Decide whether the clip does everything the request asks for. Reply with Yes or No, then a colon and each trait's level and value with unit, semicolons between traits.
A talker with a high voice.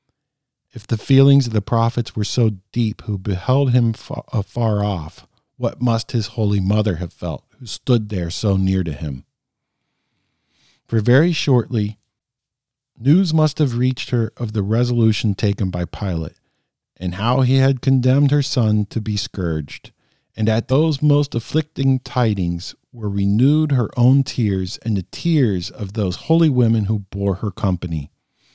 No: low, 115 Hz